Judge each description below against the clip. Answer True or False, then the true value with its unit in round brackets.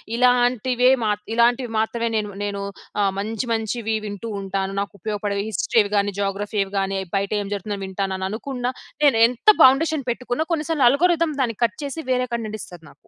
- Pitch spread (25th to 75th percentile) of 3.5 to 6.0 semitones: True (3.9 semitones)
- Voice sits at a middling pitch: False (225 Hz)